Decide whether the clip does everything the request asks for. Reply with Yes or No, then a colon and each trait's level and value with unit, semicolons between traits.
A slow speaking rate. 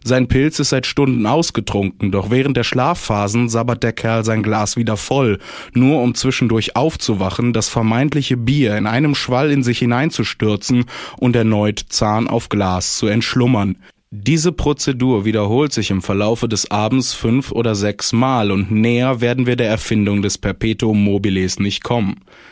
No: average, 160 wpm